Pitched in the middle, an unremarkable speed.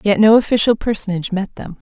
No: high, 205 Hz; average, 190 wpm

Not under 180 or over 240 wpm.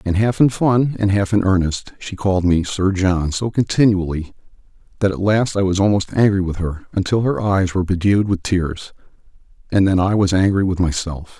Yes: average, 200 wpm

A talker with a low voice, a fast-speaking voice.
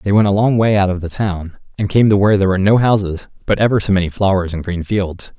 Yes: low, 100 Hz; fast, 280 wpm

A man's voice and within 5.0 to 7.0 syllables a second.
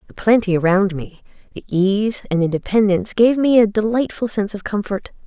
No: female; 5.5 syllables/s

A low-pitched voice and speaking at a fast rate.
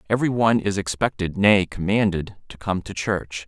No: low, 100 Hz; average, 175 wpm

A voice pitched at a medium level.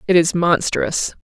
Yes: medium, 175 Hz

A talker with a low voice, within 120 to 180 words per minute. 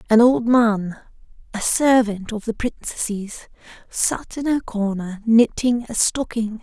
No: high, 225 Hz; slow, 135 wpm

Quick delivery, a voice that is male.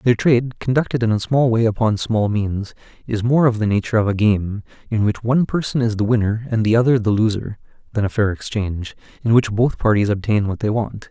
Yes: fast, 225 wpm; male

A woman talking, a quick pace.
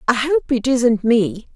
No: female; average, 195 wpm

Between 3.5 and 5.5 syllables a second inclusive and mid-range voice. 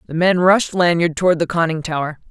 No: 5.9 syllables/s; medium, 170 Hz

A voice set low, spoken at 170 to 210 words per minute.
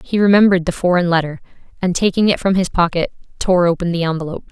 No: medium, 180 Hz; average, 200 wpm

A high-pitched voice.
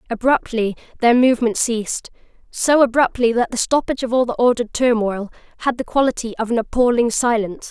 Yes: high, 240 Hz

